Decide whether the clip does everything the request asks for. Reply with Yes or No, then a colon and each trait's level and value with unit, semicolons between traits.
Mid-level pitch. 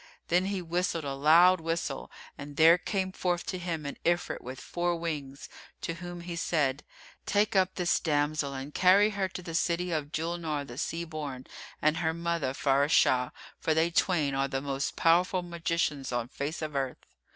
Yes: medium, 165 Hz